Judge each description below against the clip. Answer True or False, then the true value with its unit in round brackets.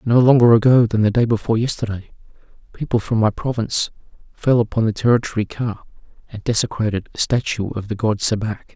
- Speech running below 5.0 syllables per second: False (6.1 syllables/s)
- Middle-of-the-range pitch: False (110 Hz)